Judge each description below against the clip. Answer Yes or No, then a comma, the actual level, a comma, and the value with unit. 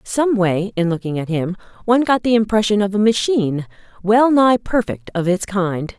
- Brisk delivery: No, average, 180 wpm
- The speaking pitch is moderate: No, high, 205 Hz